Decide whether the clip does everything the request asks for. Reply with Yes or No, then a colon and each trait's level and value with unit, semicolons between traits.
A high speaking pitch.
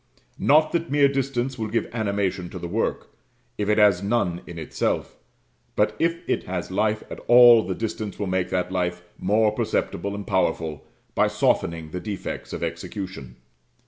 No: low, 100 Hz